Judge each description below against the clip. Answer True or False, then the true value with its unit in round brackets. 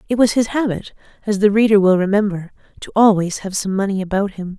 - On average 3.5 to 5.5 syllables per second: False (6.1 syllables/s)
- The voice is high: True (200 Hz)